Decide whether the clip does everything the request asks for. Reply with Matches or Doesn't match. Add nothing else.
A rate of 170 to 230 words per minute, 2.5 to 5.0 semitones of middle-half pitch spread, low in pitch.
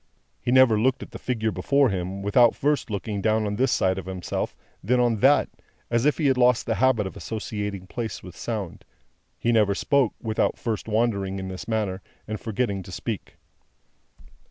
Matches